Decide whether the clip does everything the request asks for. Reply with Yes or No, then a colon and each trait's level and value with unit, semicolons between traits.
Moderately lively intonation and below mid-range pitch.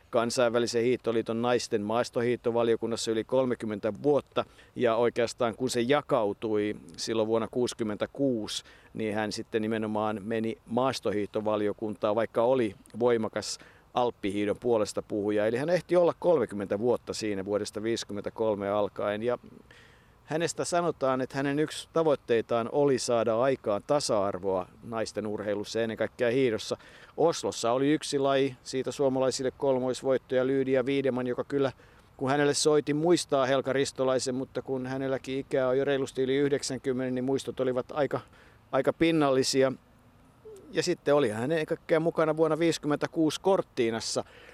Yes: average, 3.6 semitones; low, 125 Hz